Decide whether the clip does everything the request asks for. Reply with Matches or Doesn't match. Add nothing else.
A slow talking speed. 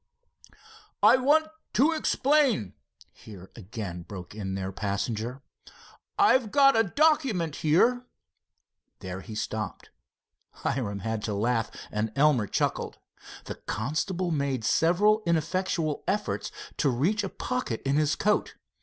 Matches